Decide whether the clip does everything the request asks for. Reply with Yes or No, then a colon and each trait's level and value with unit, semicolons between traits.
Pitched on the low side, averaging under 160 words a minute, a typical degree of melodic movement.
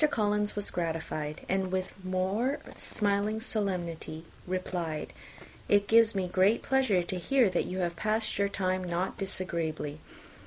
No: medium, 185 Hz; average, 150 wpm; average, 3.1 semitones